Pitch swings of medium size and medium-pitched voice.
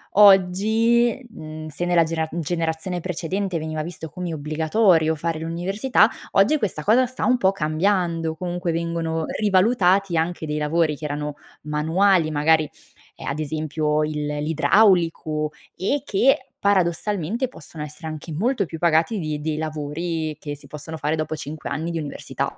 Yes: average, 3.7 semitones; medium, 165 Hz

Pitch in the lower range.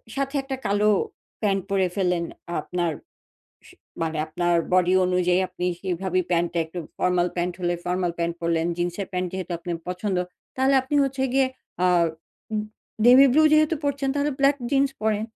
No: medium, 185 Hz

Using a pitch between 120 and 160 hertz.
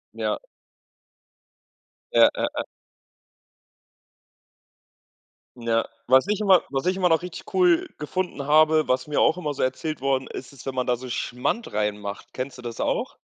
Yes: medium, 140 Hz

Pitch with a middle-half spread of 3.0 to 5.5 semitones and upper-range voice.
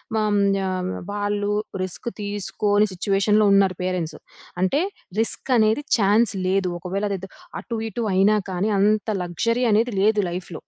No: narrow, 2.4 semitones; high, 205 Hz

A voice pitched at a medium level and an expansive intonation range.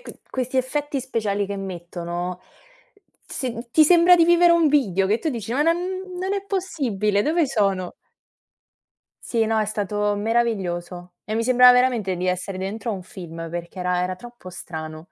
No: high, 215 Hz; wide, 6.1 semitones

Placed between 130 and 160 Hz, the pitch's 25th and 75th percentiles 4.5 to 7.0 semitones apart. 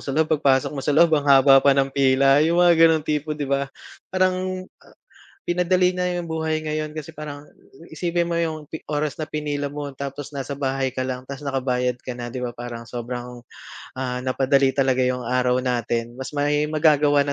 No: medium, 140 Hz; average, 3.0 semitones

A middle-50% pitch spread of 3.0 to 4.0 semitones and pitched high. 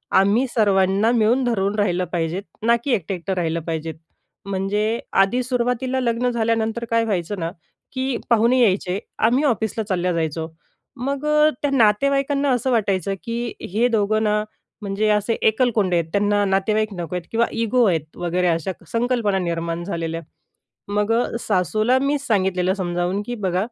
No: average, 4.4 semitones; high, 210 Hz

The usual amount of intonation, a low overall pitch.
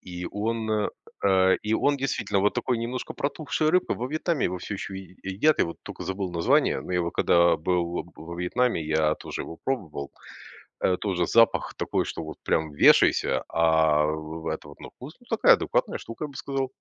No: wide, 5.9 semitones; very low, 95 Hz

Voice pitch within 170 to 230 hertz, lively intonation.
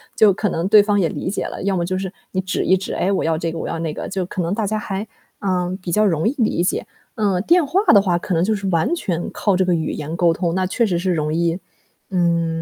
No: medium, 185 Hz; average, 3.0 semitones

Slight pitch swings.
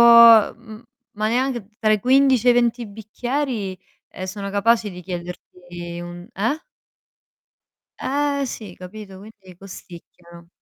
No: average, 4.4 semitones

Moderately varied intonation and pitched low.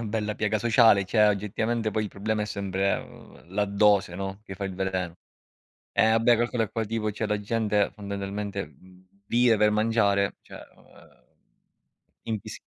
No: narrow, 2.0 semitones; low, 105 Hz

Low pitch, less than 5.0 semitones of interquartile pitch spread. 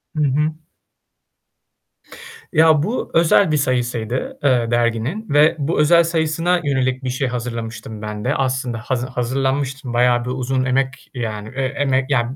Yes: low, 130 Hz; average, 3.4 semitones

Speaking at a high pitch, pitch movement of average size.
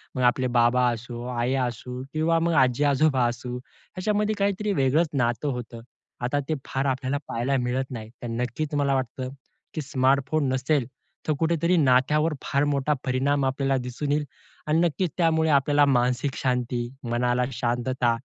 No: low, 130 Hz; average, 3.3 semitones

